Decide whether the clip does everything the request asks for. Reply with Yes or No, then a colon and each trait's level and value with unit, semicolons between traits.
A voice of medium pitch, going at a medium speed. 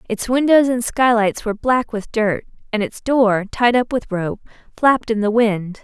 No: high, 225 Hz; average, 195 wpm